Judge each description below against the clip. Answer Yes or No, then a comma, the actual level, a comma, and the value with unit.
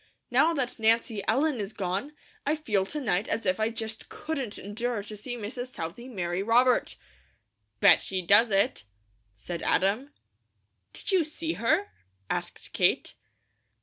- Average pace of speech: Yes, average, 150 wpm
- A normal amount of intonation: Yes, average, 4.7 semitones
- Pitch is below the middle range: No, high, 225 Hz